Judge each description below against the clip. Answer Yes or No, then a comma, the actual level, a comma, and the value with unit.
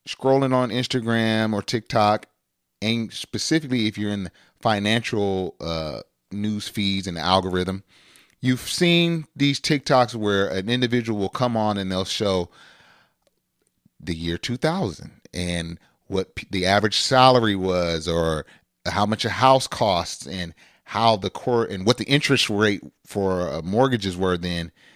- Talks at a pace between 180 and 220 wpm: No, average, 145 wpm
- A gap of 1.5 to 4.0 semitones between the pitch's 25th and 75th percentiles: No, average, 4.7 semitones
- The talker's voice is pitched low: Yes, low, 105 Hz